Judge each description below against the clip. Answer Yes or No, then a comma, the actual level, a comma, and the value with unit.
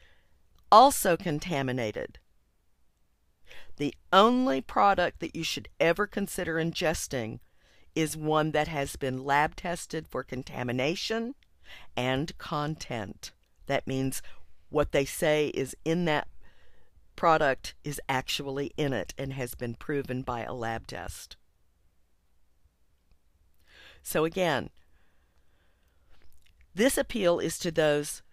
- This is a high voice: No, low, 135 Hz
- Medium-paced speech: No, slow, 105 wpm